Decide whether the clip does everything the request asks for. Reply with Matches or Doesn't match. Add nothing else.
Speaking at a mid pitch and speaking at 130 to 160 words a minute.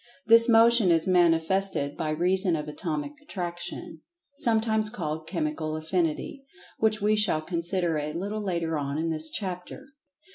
Matches